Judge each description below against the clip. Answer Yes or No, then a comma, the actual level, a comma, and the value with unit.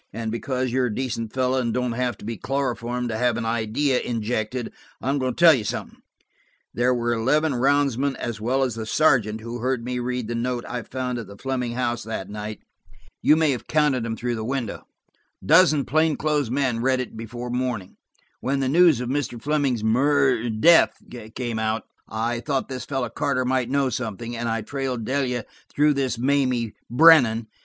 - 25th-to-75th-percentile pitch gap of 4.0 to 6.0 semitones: No, average, 2.7 semitones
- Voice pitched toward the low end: Yes, low, 125 Hz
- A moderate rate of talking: Yes, average, 190 wpm